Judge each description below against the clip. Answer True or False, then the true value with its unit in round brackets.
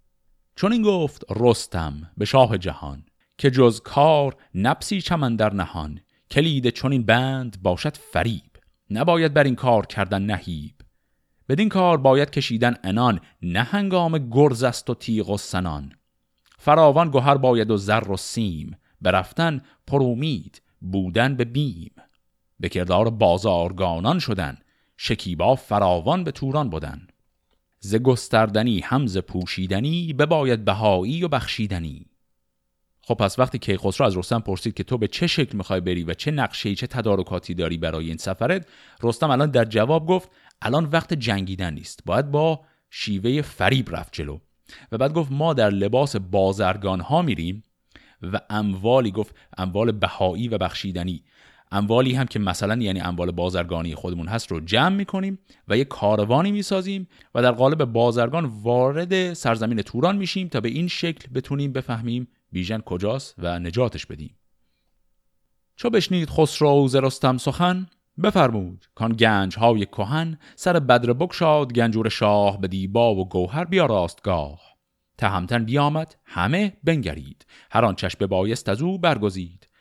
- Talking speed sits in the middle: True (145 wpm)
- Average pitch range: False (7.1 semitones)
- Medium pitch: False (115 Hz)